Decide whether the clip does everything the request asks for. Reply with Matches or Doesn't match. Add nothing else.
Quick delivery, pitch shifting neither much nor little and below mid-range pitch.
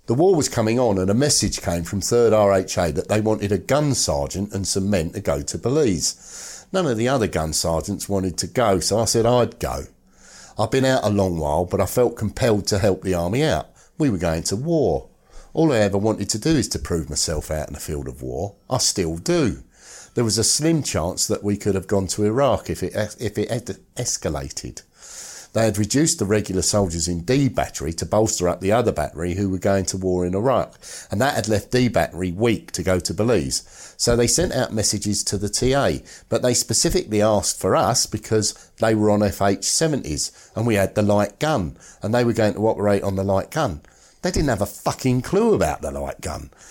Matches